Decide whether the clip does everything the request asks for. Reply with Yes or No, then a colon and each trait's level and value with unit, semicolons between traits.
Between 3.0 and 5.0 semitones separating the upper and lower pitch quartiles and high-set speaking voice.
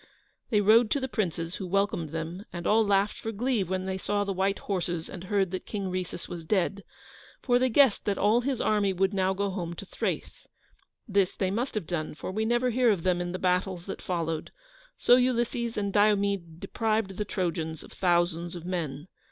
Yes: average, 3.4 semitones; high, 195 Hz